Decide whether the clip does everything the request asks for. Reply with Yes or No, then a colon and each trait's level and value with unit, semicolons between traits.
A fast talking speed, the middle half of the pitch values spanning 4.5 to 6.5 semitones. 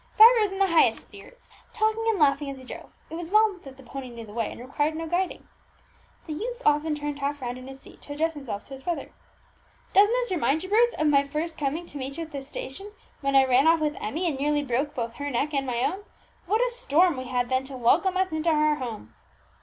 Yes: fast, 250 wpm; average, 5.1 semitones